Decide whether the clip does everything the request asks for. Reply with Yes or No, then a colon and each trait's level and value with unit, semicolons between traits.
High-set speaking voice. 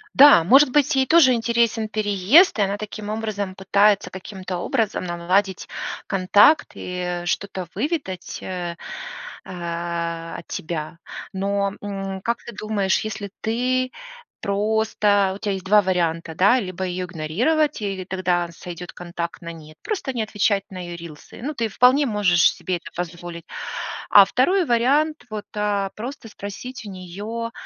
Yes: high, 200 Hz